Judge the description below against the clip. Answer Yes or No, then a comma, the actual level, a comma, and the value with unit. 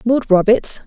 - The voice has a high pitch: Yes, high, 225 Hz